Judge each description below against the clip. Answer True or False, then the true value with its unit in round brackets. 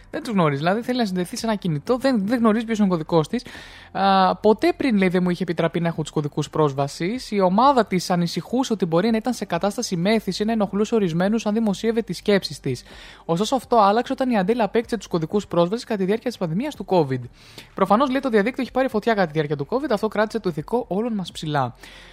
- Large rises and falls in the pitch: False (4.7 semitones)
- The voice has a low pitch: False (205 Hz)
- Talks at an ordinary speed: False (220 wpm)